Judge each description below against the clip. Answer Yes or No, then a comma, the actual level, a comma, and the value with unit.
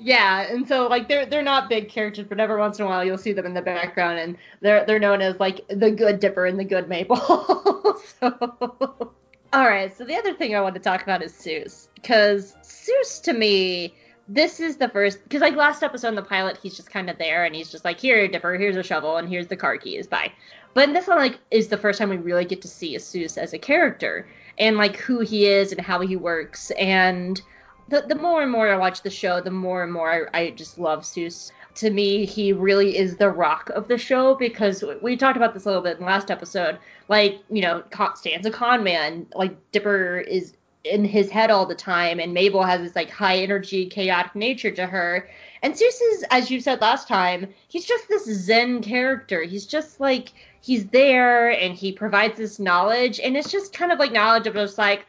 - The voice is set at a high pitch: Yes, high, 205 Hz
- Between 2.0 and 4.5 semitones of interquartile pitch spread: No, average, 4.9 semitones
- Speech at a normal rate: No, fast, 230 wpm